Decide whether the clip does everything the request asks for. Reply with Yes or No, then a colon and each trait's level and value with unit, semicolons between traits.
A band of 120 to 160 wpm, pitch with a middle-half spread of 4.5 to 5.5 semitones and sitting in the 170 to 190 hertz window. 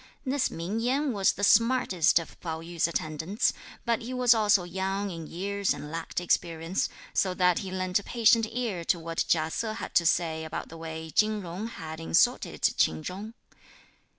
No: average, 180 wpm; average, 4.8 semitones; medium, 185 Hz